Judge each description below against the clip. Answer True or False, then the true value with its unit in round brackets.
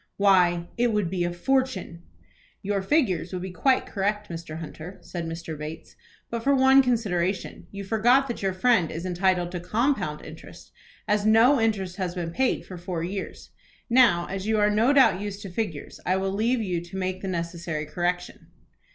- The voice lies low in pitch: False (190 Hz)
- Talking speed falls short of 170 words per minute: False (185 wpm)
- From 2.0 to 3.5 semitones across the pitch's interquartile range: False (4.2 semitones)